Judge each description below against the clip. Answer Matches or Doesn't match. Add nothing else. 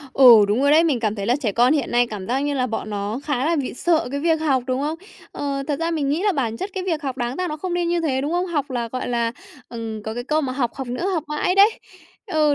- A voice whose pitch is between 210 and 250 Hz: Doesn't match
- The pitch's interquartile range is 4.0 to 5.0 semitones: Matches